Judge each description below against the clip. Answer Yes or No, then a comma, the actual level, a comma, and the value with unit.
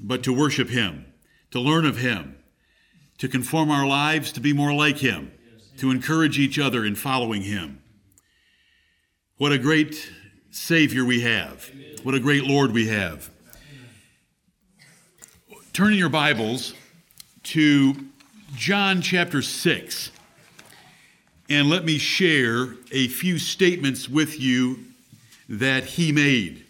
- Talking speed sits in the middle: No, slow, 125 wpm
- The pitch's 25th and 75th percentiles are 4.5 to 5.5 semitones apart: No, average, 3.7 semitones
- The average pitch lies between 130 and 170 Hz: Yes, low, 135 Hz